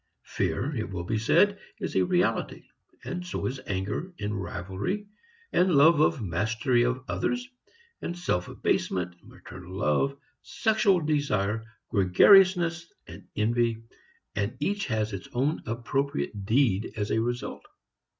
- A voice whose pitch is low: Yes, low, 120 Hz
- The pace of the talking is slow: Yes, slow, 130 wpm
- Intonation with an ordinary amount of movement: No, wide, 8.5 semitones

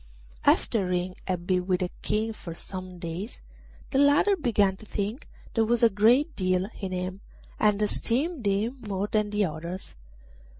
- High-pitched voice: Yes, high, 205 Hz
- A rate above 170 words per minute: No, average, 165 wpm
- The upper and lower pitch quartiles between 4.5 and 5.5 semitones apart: No, average, 3.7 semitones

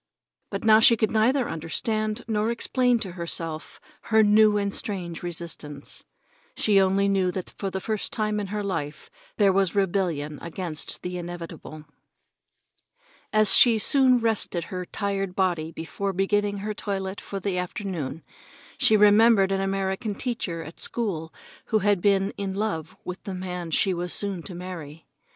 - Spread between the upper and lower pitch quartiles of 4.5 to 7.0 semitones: No, average, 3.3 semitones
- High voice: Yes, high, 195 Hz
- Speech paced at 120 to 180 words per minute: Yes, average, 155 wpm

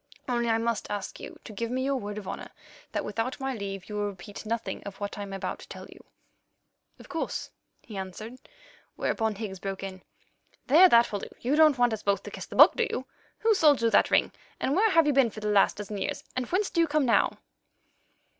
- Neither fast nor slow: No, fast, 235 wpm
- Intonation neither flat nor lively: Yes, average, 4.8 semitones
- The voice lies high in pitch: Yes, high, 230 Hz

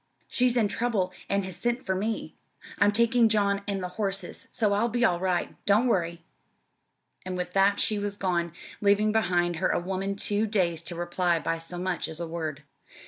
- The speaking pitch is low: No, high, 195 Hz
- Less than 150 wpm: No, average, 195 wpm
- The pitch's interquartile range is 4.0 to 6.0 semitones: No, average, 3.3 semitones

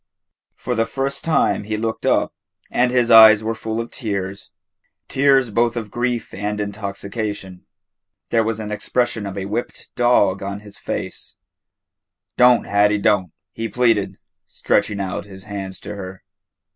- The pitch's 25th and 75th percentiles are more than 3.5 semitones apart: No, average, 2.8 semitones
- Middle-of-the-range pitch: No, low, 105 Hz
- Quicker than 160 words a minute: No, average, 155 wpm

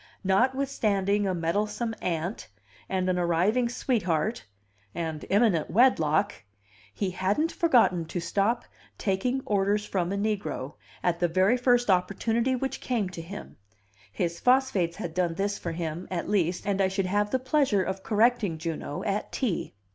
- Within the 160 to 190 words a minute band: No, average, 150 wpm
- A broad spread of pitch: No, average, 4.6 semitones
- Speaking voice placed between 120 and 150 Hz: No, high, 195 Hz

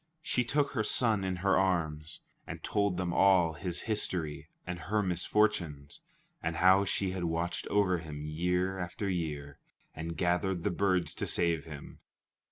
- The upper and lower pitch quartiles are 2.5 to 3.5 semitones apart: Yes, average, 2.9 semitones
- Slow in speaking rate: No, average, 160 wpm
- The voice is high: No, very low, 90 Hz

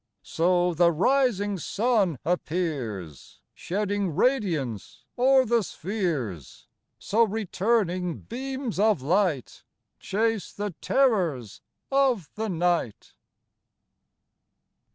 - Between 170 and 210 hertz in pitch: Yes, high, 190 Hz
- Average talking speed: No, slow, 80 wpm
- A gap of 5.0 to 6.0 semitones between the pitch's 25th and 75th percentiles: Yes, wide, 5.5 semitones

